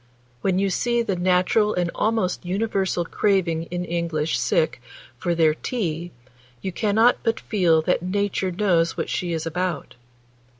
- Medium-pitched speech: Yes, medium, 180 Hz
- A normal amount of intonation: Yes, average, 3.2 semitones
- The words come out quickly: No, average, 145 wpm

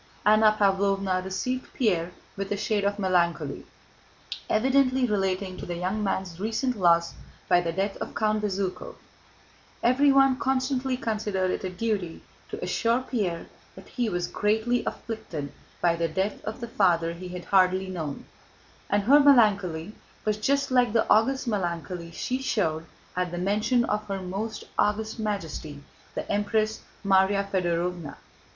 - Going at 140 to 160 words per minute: Yes, average, 145 wpm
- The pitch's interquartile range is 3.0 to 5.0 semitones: Yes, average, 3.7 semitones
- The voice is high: Yes, high, 200 Hz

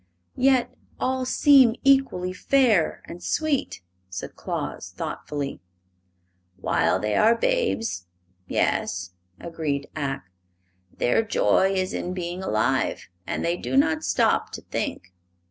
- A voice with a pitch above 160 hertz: Yes, medium, 185 Hz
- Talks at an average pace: No, slow, 115 wpm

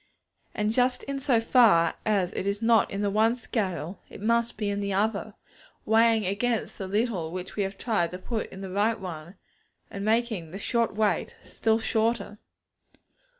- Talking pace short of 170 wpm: No, average, 180 wpm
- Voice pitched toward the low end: No, high, 210 Hz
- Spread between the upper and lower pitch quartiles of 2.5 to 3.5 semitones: Yes, average, 2.9 semitones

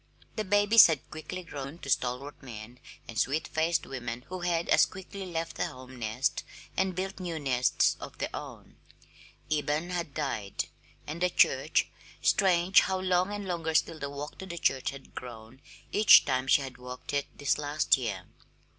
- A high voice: No, medium, 150 Hz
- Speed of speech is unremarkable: Yes, average, 175 wpm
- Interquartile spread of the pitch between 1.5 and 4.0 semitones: No, wide, 5.6 semitones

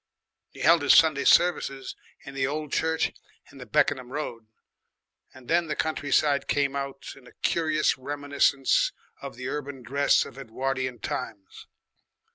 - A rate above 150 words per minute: No, average, 145 wpm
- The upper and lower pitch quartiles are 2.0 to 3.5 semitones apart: Yes, narrow, 2.4 semitones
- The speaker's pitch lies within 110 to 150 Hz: Yes, medium, 140 Hz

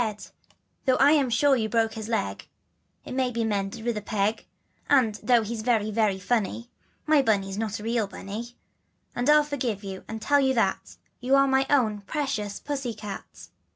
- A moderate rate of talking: Yes, average, 175 wpm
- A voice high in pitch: Yes, high, 230 Hz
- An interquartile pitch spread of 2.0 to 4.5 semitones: Yes, average, 3.8 semitones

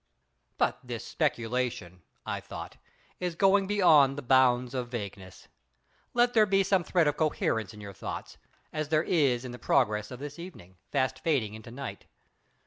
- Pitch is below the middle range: Yes, low, 130 Hz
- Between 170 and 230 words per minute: No, average, 155 wpm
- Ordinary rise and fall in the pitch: No, wide, 6.1 semitones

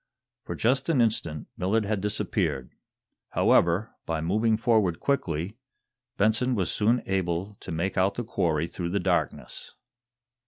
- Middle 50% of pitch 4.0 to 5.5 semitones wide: Yes, average, 4.5 semitones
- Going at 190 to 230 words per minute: No, slow, 135 wpm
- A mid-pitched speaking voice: No, low, 100 Hz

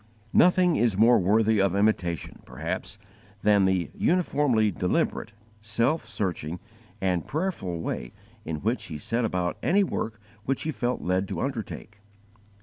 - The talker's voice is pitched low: Yes, low, 105 Hz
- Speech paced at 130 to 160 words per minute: Yes, average, 140 wpm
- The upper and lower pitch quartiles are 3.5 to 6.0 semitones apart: Yes, average, 5.1 semitones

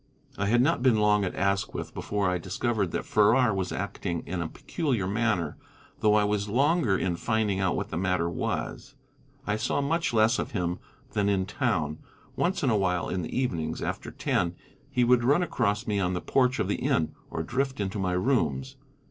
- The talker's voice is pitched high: No, low, 105 Hz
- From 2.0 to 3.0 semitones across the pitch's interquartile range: No, average, 4.7 semitones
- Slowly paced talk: No, average, 200 wpm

